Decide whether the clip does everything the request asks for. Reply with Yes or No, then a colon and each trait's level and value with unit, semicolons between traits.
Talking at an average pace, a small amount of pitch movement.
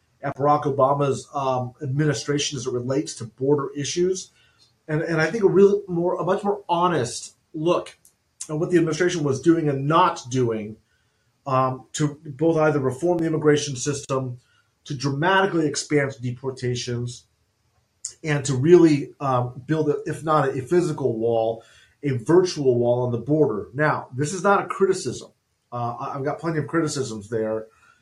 No: average, 160 wpm; average, 4.4 semitones